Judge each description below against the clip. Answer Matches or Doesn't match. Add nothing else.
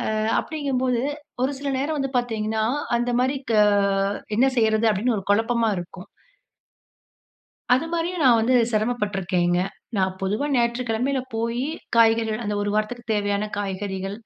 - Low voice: Doesn't match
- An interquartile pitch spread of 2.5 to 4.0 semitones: Matches